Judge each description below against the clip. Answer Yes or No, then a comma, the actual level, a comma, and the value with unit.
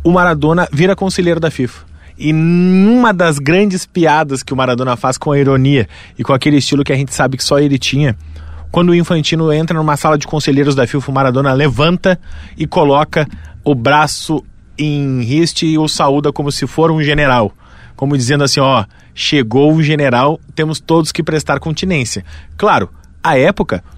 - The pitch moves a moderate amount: Yes, average, 3.3 semitones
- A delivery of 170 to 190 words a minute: Yes, fast, 185 wpm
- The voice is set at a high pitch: No, medium, 145 Hz